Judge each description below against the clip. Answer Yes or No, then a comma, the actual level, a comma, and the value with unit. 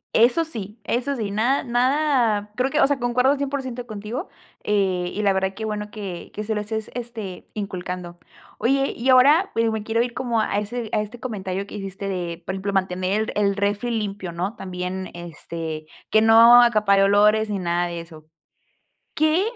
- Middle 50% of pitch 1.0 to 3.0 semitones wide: No, average, 4.0 semitones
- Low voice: No, high, 210 Hz